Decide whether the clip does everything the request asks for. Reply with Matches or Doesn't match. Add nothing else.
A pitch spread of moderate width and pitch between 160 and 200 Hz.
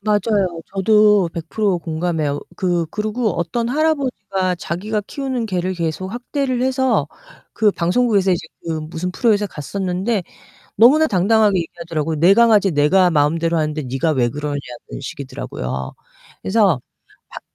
Matches